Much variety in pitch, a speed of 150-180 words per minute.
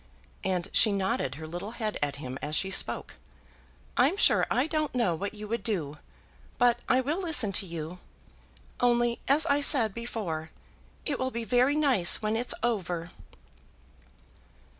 Yes: wide, 6.3 semitones; average, 160 wpm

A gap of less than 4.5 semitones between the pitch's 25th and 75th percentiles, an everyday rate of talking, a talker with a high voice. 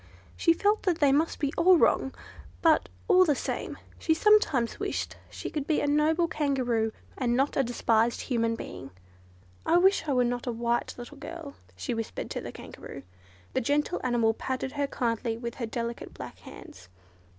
No: average, 5.0 semitones; average, 180 wpm; very high, 265 Hz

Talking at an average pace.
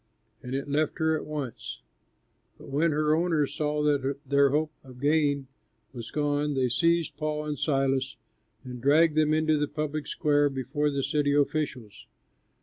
Yes: average, 160 wpm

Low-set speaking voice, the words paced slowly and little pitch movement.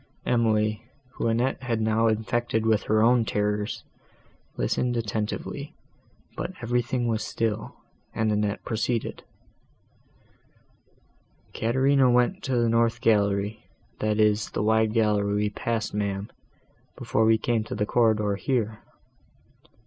Yes: low, 110 Hz; slow, 120 wpm; narrow, 1.9 semitones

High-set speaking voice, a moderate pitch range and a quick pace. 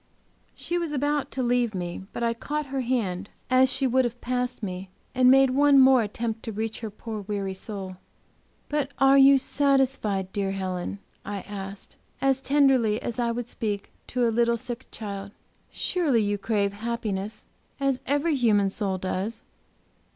No: high, 235 Hz; average, 4.6 semitones; average, 165 wpm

